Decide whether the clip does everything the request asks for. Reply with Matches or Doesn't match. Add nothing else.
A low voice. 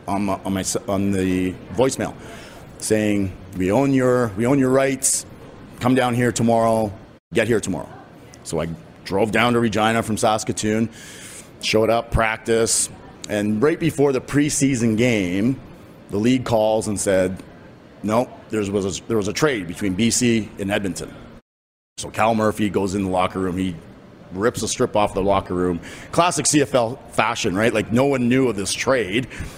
Matches